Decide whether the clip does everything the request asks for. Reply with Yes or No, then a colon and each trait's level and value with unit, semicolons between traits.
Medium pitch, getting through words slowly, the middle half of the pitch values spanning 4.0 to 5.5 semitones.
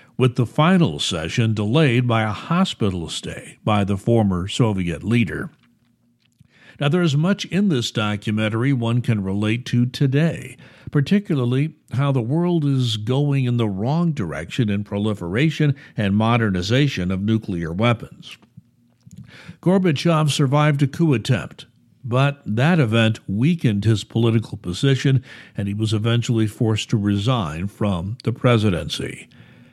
No: low, 120 Hz; slow, 130 wpm; average, 4.8 semitones